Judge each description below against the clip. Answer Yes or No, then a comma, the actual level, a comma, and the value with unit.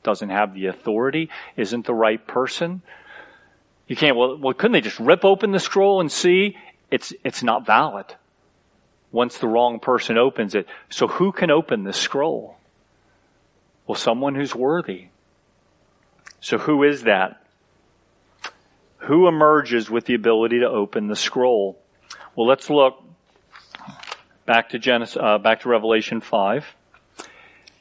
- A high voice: No, low, 120 Hz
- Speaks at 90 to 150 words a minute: Yes, average, 140 wpm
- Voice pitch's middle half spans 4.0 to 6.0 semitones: Yes, wide, 5.6 semitones